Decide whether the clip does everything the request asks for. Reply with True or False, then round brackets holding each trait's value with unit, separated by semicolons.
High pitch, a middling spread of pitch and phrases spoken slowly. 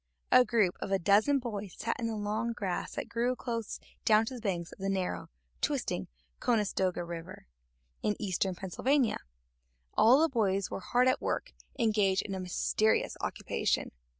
False (210 Hz; 3.6 semitones; 170 wpm)